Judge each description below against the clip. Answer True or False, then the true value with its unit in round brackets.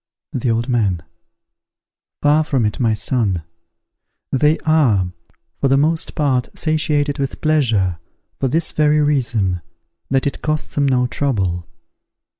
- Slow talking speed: True (130 wpm)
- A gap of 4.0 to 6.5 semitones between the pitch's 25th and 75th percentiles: True (5.4 semitones)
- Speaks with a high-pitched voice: False (135 Hz)